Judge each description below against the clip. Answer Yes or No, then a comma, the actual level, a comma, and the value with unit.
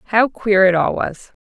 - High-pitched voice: Yes, high, 205 Hz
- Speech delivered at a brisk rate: Yes, fast, 210 wpm